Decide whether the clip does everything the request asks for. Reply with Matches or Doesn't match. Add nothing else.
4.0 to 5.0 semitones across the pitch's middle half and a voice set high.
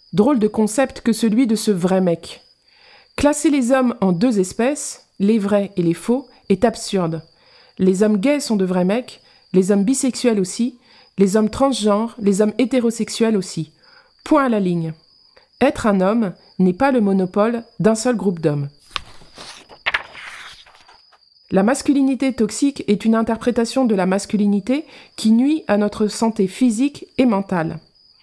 Matches